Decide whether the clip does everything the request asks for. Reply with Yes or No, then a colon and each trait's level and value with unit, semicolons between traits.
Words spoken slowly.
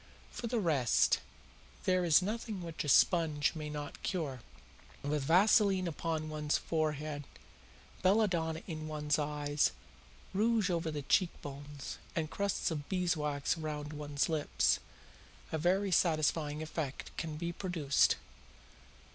Yes: slow, 125 wpm